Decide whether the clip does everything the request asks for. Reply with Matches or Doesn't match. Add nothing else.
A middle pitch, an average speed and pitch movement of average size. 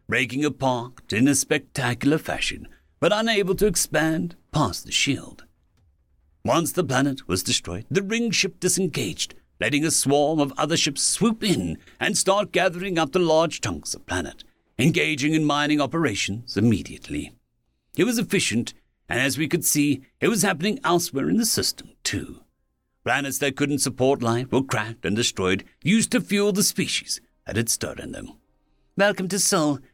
Doesn't match